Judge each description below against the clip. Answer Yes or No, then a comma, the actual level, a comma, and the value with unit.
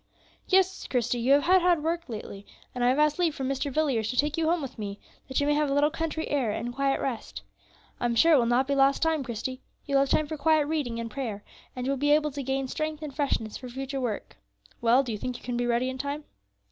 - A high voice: Yes, very high, 275 Hz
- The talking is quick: Yes, fast, 270 wpm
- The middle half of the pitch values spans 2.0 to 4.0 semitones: Yes, average, 3.7 semitones